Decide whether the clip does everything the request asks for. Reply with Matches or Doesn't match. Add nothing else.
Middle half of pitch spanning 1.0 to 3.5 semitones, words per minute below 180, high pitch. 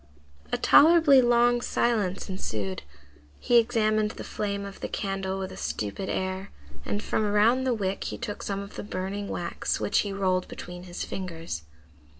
Matches